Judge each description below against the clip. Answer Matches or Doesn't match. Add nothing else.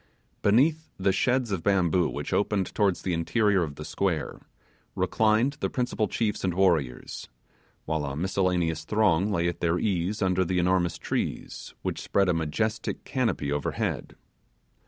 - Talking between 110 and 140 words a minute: Doesn't match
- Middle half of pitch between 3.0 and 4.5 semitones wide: Matches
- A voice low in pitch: Matches